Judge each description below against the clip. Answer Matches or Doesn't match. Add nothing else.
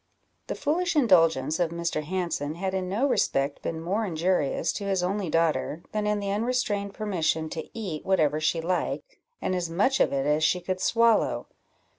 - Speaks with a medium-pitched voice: Matches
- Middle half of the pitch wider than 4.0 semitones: Matches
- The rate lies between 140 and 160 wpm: Doesn't match